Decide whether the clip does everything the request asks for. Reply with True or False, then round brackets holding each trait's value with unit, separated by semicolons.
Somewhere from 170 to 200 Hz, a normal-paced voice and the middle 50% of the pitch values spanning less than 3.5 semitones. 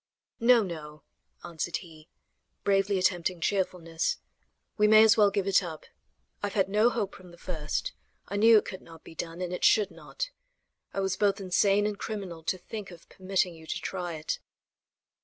True (190 Hz; 185 wpm; 3.1 semitones)